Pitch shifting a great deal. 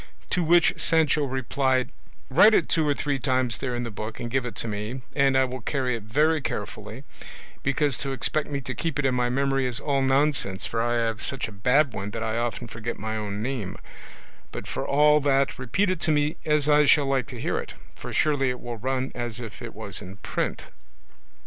No: average, 3.7 semitones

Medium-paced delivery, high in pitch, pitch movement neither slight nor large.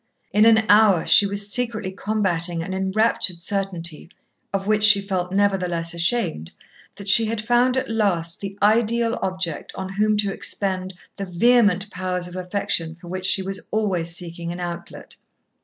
Yes: average, 160 wpm; high, 195 Hz; average, 3.2 semitones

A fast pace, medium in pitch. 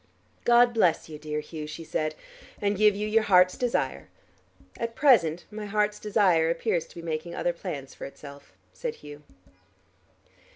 No: average, 160 wpm; medium, 175 Hz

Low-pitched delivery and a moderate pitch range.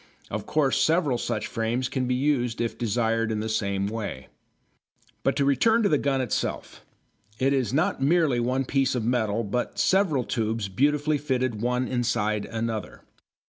Yes: low, 125 Hz; average, 3.7 semitones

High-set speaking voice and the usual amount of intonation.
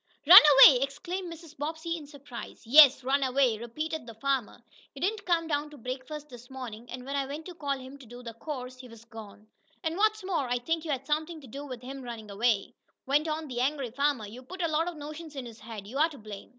Yes: very high, 275 Hz; average, 4.1 semitones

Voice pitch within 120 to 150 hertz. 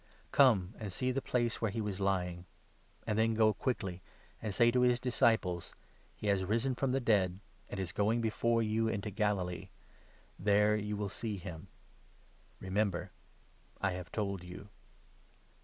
No: low, 105 Hz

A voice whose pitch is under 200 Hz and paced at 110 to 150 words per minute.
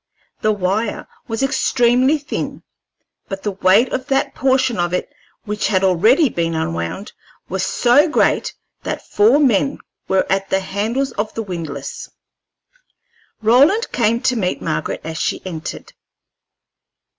No: high, 210 Hz; slow, 135 wpm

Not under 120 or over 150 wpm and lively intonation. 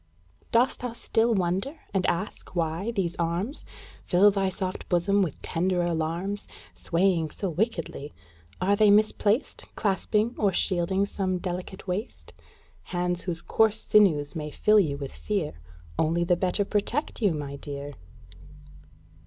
No: slow, 135 wpm; average, 3.3 semitones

